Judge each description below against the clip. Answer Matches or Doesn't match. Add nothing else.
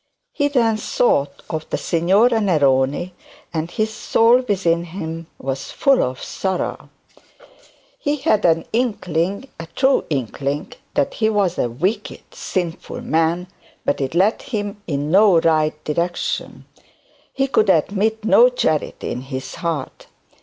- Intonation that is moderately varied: Doesn't match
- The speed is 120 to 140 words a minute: Matches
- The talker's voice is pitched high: Doesn't match